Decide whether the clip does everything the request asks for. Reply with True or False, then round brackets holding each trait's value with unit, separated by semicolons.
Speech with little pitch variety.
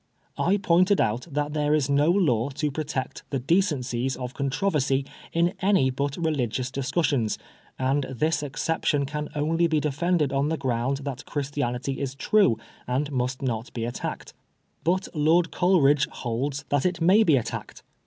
False (3.7 semitones)